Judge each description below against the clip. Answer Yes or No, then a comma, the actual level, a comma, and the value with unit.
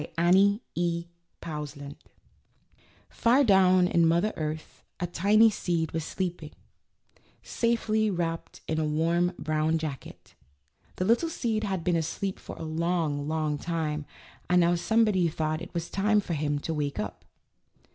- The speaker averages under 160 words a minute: Yes, average, 145 wpm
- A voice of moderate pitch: Yes, medium, 170 Hz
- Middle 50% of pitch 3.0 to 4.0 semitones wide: Yes, average, 3.5 semitones